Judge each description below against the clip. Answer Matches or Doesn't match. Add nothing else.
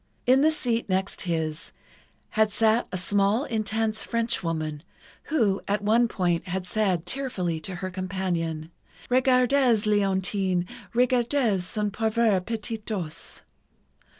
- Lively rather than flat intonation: Doesn't match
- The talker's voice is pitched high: Matches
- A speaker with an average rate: Doesn't match